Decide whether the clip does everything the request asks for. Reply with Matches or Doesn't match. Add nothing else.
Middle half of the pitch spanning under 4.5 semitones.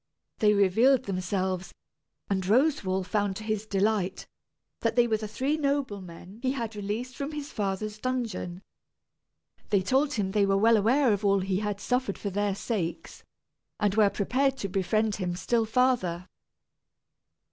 Matches